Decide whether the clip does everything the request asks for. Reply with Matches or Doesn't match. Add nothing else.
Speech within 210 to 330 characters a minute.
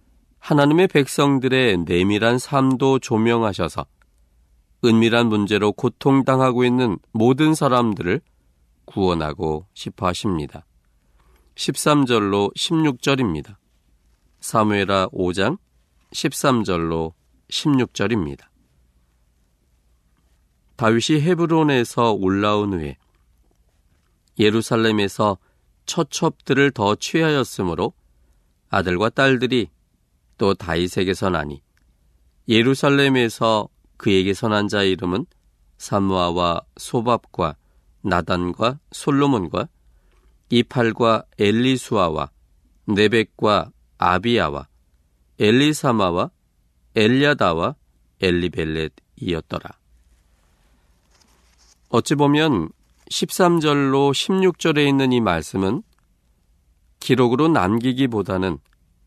Doesn't match